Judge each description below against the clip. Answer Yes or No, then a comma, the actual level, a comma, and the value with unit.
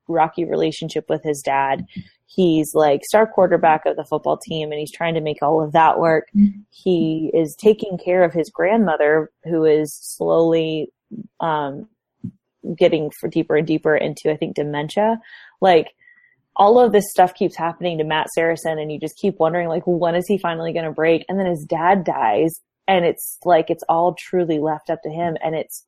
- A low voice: No, medium, 165 Hz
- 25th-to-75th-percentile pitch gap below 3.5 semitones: Yes, average, 2.8 semitones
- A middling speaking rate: Yes, average, 190 wpm